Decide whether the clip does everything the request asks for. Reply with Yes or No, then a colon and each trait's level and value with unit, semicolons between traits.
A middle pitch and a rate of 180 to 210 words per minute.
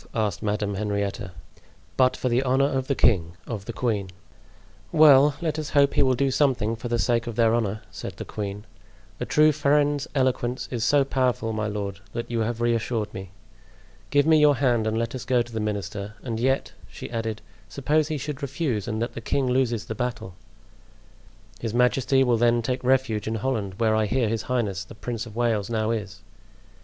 No: low, 120 Hz; average, 195 wpm